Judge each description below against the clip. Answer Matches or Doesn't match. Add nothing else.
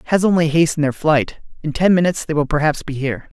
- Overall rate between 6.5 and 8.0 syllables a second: Matches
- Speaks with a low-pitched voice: Doesn't match